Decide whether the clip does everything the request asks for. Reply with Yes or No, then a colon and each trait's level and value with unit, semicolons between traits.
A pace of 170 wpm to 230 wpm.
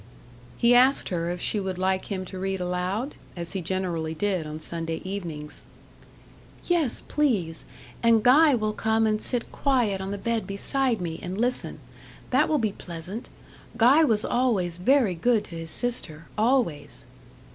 No: average, 160 wpm